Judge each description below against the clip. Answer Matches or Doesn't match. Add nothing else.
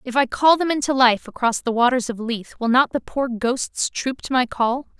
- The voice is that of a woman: Matches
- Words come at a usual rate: Doesn't match